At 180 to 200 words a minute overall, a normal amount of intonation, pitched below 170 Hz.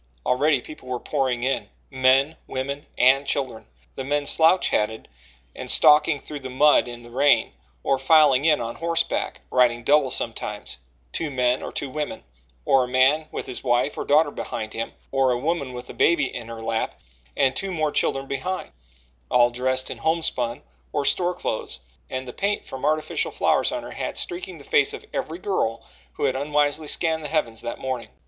Yes: average, 185 wpm; average, 3.5 semitones; low, 135 Hz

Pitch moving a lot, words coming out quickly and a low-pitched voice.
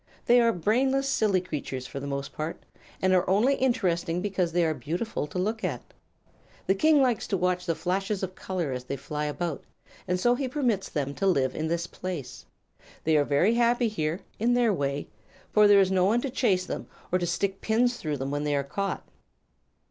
No: wide, 6.2 semitones; fast, 210 wpm; medium, 185 Hz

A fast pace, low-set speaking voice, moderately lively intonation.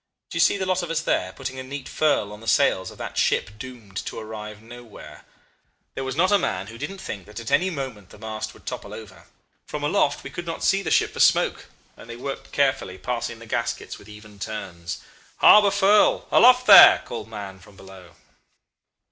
No: fast, 210 wpm; low, 115 Hz; wide, 6.6 semitones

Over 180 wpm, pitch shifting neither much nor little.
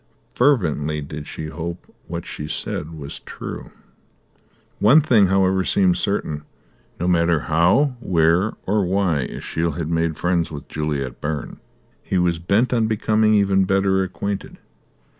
No: average, 140 wpm; average, 3.9 semitones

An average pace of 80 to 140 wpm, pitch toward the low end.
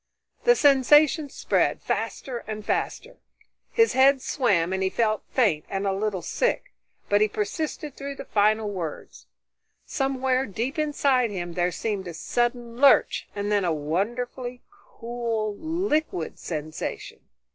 No: slow, 135 wpm; high, 230 Hz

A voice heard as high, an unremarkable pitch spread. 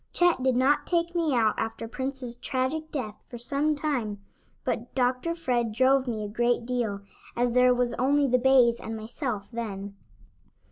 Yes: very high, 250 Hz; average, 3.0 semitones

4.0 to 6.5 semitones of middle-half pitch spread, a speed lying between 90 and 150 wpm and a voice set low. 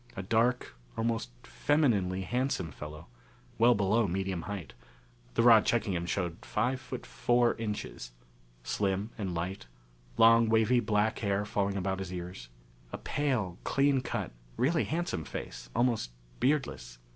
Yes: average, 4.6 semitones; slow, 135 wpm; low, 105 Hz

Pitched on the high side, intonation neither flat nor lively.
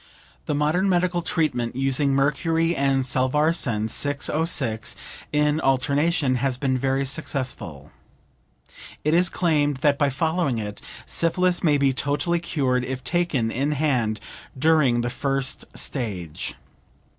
No: medium, 140 Hz; average, 3.7 semitones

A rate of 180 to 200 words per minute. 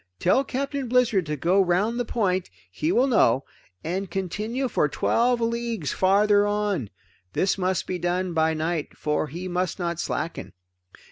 No: average, 155 wpm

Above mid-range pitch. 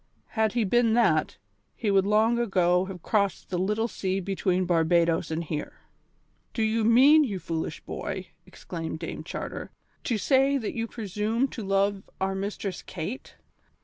Yes: high, 200 Hz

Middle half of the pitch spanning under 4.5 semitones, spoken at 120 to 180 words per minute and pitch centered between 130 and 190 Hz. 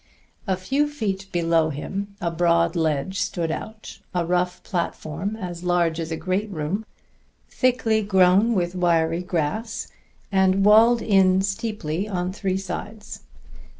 Yes: average, 3.4 semitones; slow, 135 wpm; medium, 185 Hz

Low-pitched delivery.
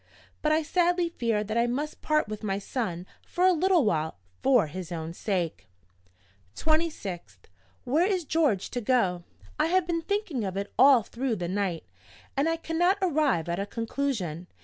No: high, 245 Hz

